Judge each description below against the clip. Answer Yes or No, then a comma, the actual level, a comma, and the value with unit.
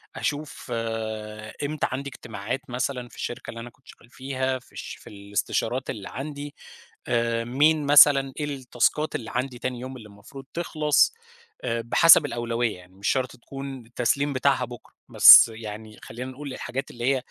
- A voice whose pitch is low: Yes, low, 125 Hz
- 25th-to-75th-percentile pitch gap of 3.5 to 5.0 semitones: No, average, 3.1 semitones